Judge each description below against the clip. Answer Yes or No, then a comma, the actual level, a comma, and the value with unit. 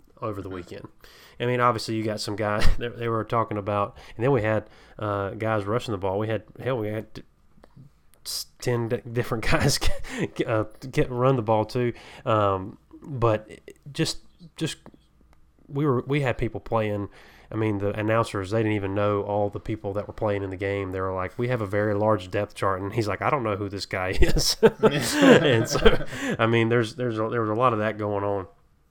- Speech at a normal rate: No, fast, 210 wpm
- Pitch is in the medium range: No, low, 110 Hz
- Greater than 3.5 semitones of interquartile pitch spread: No, average, 2.8 semitones